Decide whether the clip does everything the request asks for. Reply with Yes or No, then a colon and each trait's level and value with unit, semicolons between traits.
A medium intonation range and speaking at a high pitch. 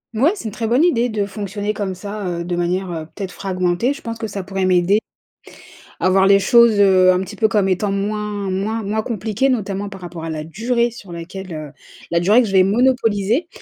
Yes: average, 3.1 semitones; high, 200 Hz